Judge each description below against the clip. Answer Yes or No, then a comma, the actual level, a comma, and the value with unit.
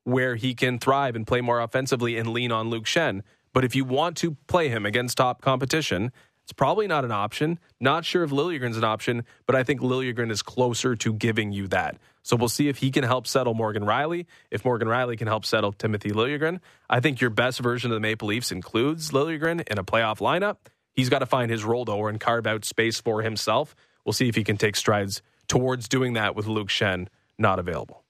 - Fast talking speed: Yes, fast, 225 wpm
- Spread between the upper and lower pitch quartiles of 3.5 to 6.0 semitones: No, average, 3.1 semitones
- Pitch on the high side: No, low, 120 Hz